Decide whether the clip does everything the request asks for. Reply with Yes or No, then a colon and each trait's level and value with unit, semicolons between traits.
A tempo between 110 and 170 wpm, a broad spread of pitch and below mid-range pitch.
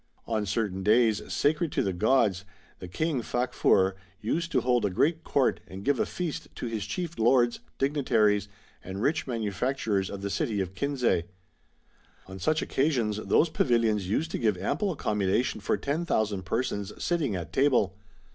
Yes: average, 165 wpm; wide, 5.9 semitones; low, 115 Hz